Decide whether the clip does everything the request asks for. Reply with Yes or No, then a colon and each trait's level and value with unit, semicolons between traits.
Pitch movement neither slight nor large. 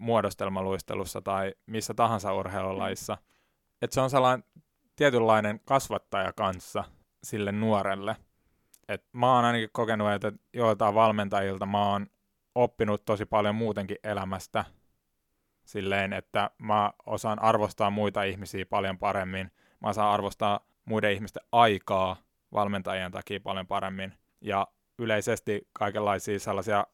No: narrow, 2.1 semitones